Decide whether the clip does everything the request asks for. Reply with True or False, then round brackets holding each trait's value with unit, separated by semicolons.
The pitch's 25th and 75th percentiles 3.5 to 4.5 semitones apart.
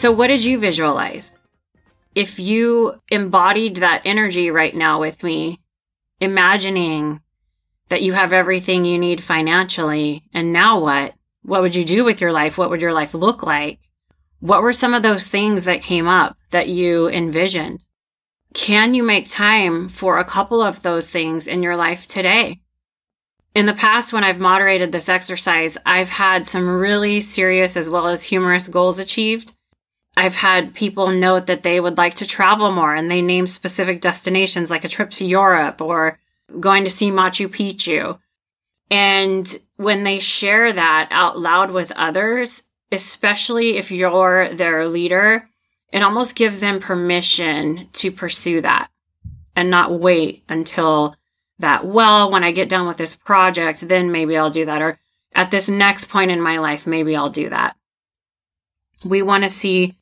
False (3.0 semitones)